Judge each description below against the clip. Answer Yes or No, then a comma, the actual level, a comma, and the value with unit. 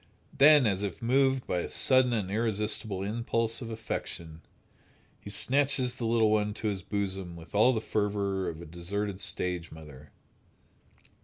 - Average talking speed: Yes, average, 155 wpm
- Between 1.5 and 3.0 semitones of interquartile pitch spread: No, average, 3.9 semitones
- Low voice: Yes, low, 105 Hz